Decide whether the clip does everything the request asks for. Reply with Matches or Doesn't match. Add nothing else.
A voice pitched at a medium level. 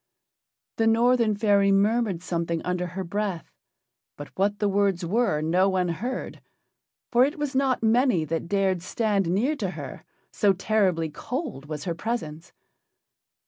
Doesn't match